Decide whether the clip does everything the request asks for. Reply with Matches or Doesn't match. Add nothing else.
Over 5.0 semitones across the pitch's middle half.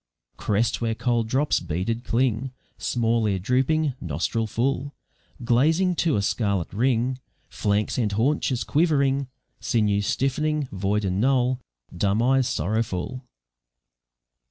Doesn't match